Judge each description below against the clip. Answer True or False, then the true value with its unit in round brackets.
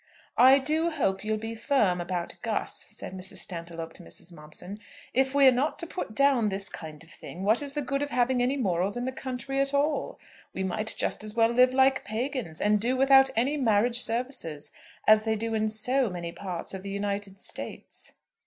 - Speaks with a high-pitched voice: True (225 Hz)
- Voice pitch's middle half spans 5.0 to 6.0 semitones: True (5.6 semitones)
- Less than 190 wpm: False (200 wpm)